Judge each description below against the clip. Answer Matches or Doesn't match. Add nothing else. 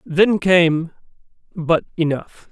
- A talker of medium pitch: Matches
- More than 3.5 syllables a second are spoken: Doesn't match